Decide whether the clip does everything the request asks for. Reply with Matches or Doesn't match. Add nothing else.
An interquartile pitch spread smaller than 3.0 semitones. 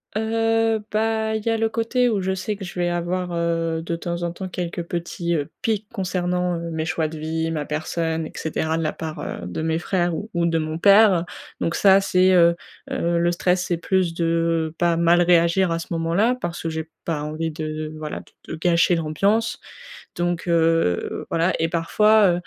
Matches